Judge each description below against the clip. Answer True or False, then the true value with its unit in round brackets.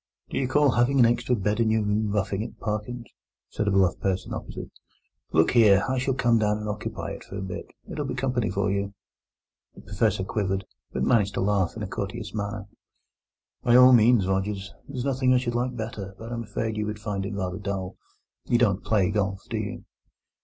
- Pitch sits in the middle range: False (105 Hz)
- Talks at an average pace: False (210 wpm)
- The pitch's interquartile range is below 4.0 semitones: True (3.5 semitones)